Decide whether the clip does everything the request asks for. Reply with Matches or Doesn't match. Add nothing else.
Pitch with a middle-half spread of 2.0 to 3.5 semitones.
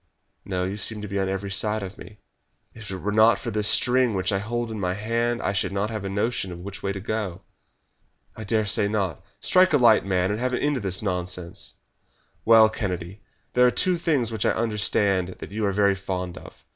Matches